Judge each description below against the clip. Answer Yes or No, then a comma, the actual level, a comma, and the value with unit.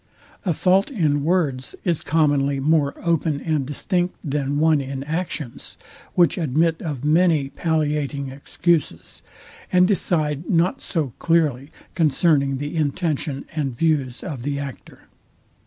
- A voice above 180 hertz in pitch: No, medium, 150 Hz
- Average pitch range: Yes, average, 3.1 semitones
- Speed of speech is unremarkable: No, slow, 125 wpm